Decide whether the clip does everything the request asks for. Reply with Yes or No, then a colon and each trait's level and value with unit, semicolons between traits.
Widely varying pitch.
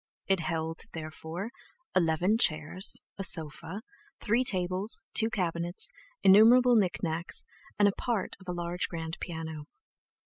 No: average, 3.8 semitones